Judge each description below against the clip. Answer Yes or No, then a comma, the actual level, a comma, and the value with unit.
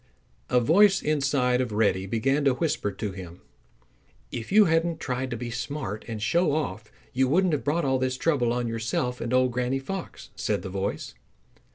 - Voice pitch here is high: No, low, 125 Hz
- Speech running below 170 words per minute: No, average, 185 wpm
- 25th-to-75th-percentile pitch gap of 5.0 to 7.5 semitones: No, average, 4.6 semitones